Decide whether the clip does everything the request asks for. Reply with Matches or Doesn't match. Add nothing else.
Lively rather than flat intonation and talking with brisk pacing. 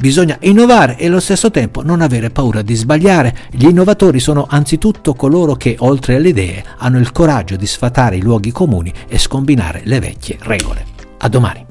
Matches